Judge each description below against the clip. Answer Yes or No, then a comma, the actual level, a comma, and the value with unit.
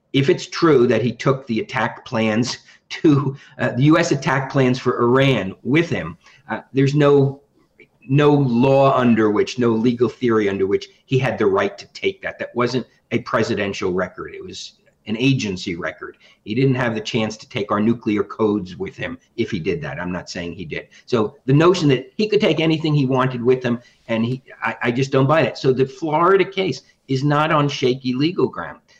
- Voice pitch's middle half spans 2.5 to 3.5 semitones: No, average, 3.9 semitones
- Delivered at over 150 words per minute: Yes, fast, 205 wpm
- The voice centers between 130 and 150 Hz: Yes, low, 135 Hz